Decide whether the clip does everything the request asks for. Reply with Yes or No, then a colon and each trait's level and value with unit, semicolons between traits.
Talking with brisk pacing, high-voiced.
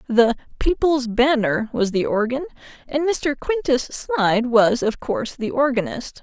No: average, 145 wpm; very high, 250 Hz